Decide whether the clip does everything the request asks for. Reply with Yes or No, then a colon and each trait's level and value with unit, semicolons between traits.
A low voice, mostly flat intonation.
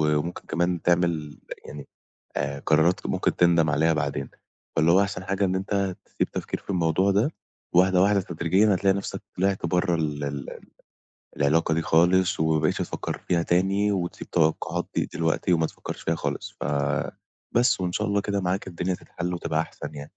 No: very low, 90 Hz; average, 3.1 semitones